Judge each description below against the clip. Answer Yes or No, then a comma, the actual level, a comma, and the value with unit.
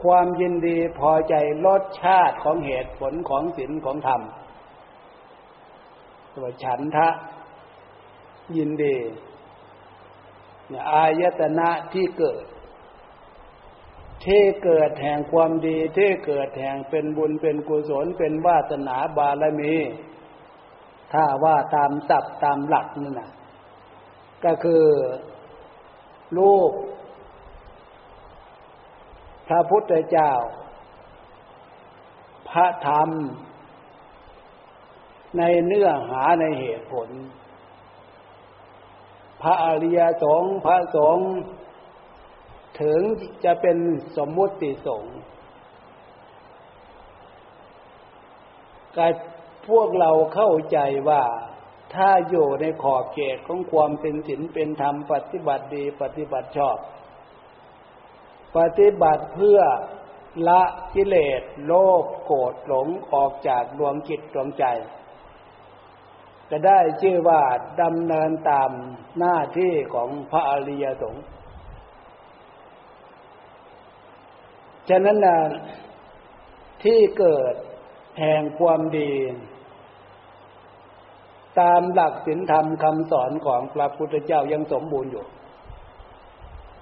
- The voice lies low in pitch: No, medium, 160 Hz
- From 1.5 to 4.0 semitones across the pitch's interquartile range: Yes, average, 3.2 semitones